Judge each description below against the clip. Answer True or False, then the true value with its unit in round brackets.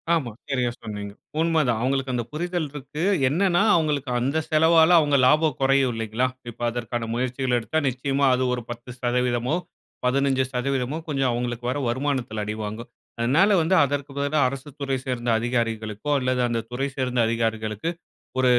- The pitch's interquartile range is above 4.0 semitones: False (3.1 semitones)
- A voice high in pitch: False (130 Hz)